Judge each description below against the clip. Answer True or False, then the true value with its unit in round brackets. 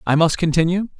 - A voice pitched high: False (170 Hz)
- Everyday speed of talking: True (180 wpm)